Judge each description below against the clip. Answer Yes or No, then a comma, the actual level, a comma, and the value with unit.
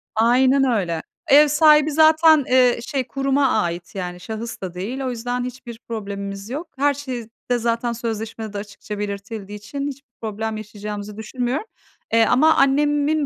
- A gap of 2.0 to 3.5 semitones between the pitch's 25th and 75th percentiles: No, average, 4.7 semitones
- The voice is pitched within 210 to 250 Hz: Yes, high, 235 Hz